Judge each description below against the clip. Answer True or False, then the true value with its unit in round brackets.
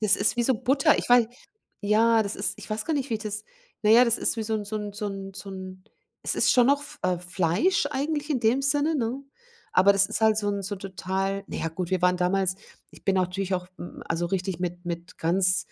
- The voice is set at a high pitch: True (200 Hz)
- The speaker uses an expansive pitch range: False (3.8 semitones)